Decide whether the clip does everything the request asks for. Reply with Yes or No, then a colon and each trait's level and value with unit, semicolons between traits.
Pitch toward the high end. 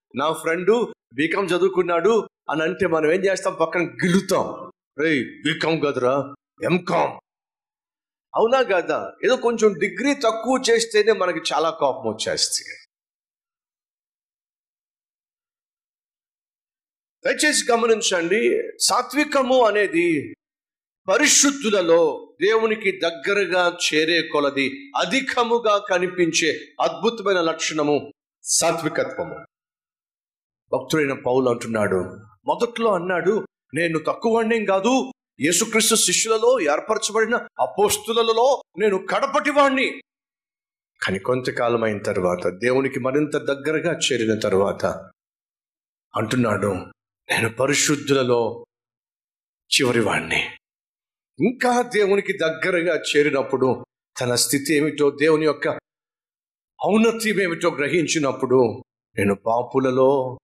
No: medium, 180 Hz